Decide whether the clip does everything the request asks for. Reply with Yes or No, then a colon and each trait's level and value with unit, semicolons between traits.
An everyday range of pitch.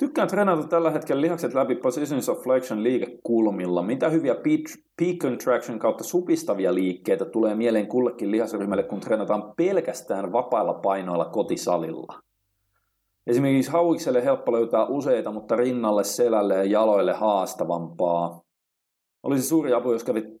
No: wide, 7.7 semitones